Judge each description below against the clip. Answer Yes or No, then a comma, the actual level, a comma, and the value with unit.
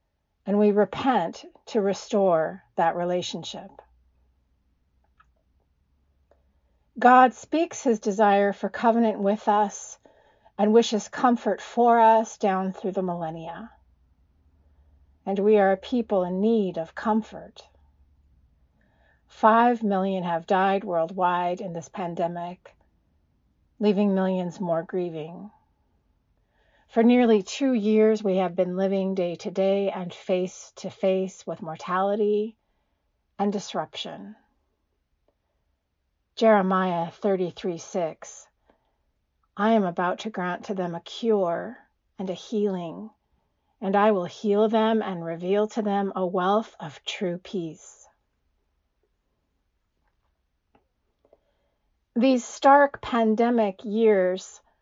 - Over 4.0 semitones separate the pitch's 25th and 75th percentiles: Yes, average, 5.1 semitones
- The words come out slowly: Yes, slow, 105 wpm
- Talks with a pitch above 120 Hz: Yes, high, 190 Hz